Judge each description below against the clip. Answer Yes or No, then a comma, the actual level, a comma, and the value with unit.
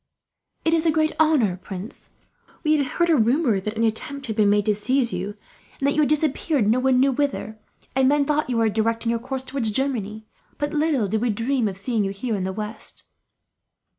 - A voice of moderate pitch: No, high, 245 Hz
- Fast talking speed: Yes, fast, 225 wpm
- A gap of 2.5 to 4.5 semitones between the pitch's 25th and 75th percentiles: No, average, 4.9 semitones